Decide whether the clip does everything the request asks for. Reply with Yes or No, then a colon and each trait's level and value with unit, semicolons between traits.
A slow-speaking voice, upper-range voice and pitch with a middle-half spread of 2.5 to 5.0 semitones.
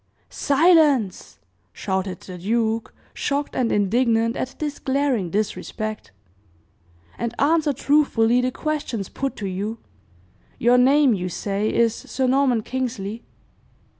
Yes: slow, 115 wpm; high, 235 Hz; average, 4.6 semitones